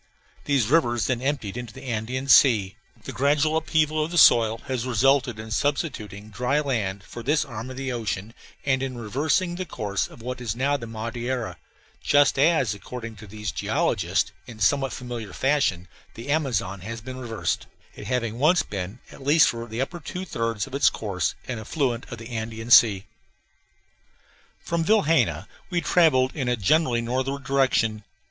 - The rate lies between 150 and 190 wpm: Yes, average, 170 wpm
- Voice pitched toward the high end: No, low, 125 Hz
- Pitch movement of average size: Yes, average, 4.2 semitones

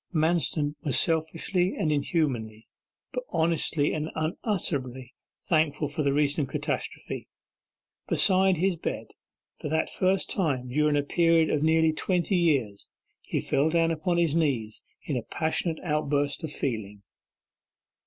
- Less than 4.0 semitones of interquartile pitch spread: Yes, average, 2.8 semitones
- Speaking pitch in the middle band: Yes, medium, 155 Hz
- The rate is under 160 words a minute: Yes, slow, 135 wpm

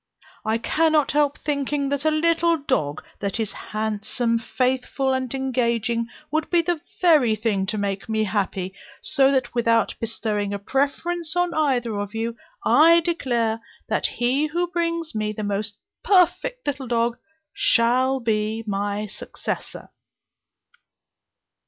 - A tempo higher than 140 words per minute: No, slow, 135 wpm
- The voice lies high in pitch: Yes, high, 245 Hz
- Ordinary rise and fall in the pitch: No, wide, 5.9 semitones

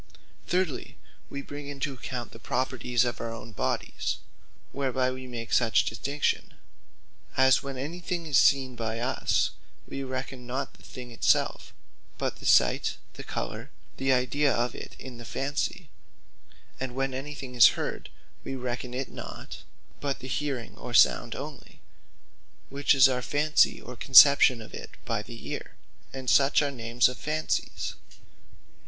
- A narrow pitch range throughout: Yes, narrow, 2.3 semitones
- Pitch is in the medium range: No, low, 130 Hz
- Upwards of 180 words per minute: No, average, 160 wpm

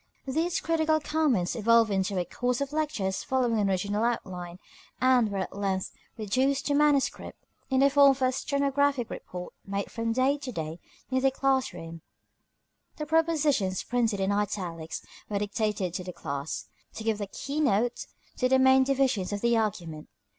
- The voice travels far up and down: Yes, wide, 5.9 semitones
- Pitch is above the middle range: Yes, high, 230 Hz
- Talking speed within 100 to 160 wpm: No, average, 170 wpm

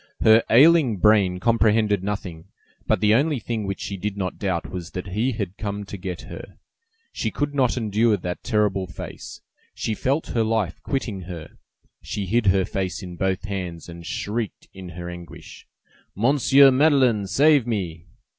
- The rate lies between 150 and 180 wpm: Yes, average, 165 wpm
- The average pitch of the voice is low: Yes, low, 105 Hz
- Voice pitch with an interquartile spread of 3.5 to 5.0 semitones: Yes, average, 4.1 semitones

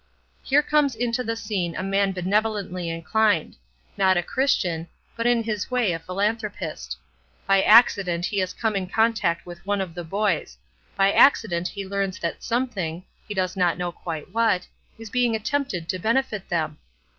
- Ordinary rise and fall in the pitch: Yes, average, 4.3 semitones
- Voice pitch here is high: Yes, high, 195 Hz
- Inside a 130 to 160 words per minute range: No, average, 170 wpm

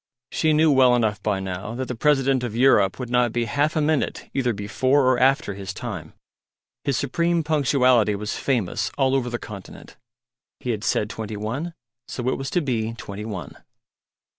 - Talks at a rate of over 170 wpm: Yes, average, 185 wpm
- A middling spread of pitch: Yes, average, 4.3 semitones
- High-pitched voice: No, low, 125 Hz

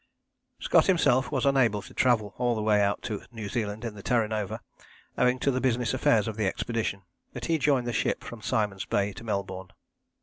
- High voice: No, low, 115 Hz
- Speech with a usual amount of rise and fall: Yes, average, 3.3 semitones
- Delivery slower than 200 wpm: No, fast, 205 wpm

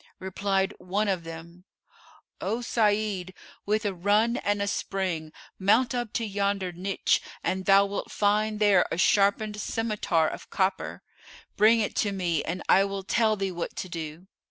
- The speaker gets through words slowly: No, average, 160 wpm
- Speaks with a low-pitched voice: No, high, 200 Hz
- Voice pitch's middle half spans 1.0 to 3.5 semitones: Yes, narrow, 2.4 semitones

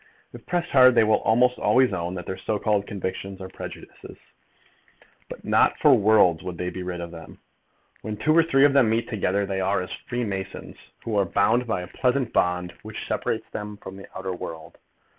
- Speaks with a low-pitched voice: Yes, low, 100 Hz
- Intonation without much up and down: No, average, 4.4 semitones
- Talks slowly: No, average, 200 wpm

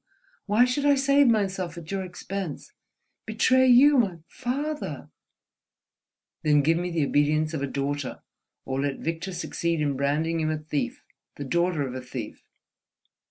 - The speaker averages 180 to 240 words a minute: No, average, 145 wpm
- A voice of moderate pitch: Yes, medium, 170 Hz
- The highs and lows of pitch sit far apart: Yes, wide, 7.0 semitones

